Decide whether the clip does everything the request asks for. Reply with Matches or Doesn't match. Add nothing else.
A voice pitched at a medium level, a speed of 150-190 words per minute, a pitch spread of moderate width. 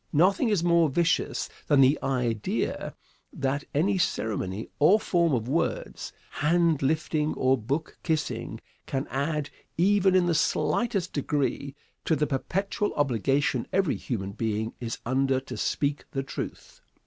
Doesn't match